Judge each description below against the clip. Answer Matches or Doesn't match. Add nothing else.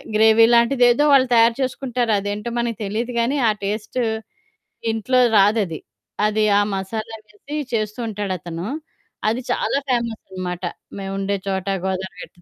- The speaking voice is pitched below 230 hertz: Matches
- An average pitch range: Matches